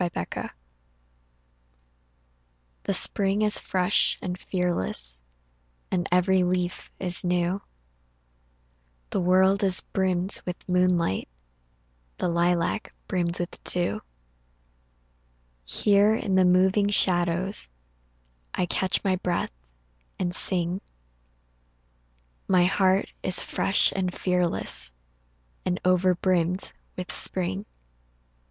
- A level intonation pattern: Yes, narrow, 1.3 semitones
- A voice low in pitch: No, medium, 180 Hz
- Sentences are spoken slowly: Yes, slow, 95 wpm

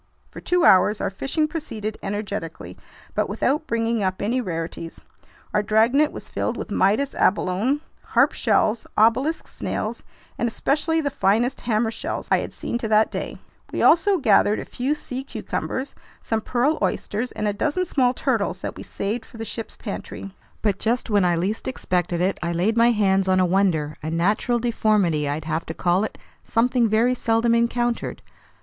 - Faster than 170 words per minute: Yes, average, 180 wpm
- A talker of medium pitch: No, high, 220 Hz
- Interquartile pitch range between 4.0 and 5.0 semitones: Yes, average, 4.3 semitones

